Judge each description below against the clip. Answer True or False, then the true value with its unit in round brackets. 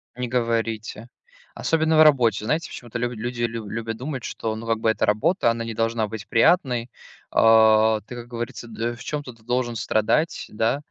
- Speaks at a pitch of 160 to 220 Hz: False (115 Hz)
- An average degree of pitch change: False (1.9 semitones)